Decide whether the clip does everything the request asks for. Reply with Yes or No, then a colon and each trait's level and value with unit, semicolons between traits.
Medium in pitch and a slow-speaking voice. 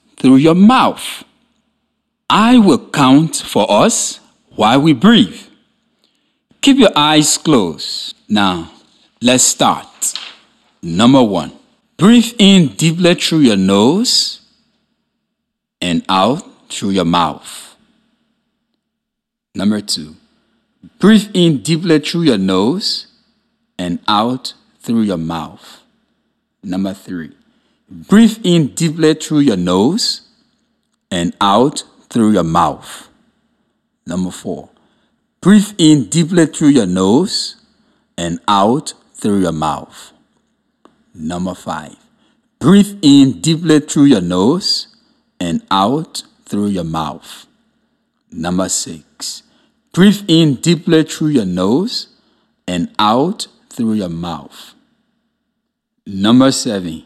Yes: medium, 170 Hz; slow, 105 wpm